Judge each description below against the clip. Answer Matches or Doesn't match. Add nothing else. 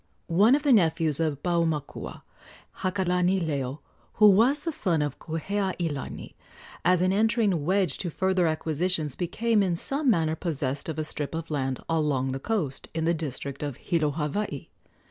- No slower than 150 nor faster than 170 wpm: Matches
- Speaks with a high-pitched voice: Doesn't match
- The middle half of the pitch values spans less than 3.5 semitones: Doesn't match